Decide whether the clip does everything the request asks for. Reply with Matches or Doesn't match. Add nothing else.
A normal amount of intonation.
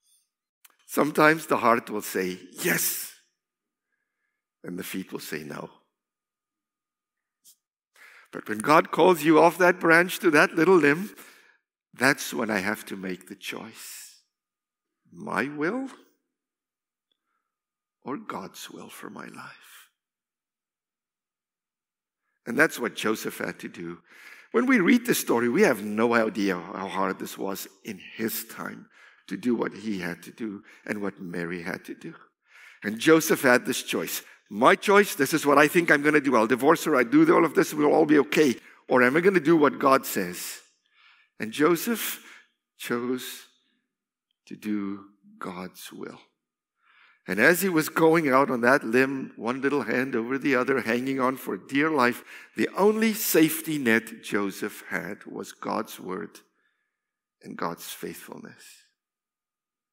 Doesn't match